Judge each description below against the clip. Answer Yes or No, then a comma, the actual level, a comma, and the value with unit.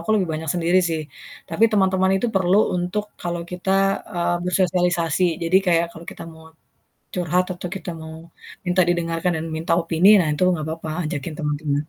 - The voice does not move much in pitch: Yes, narrow, 2.0 semitones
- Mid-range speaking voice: Yes, medium, 175 Hz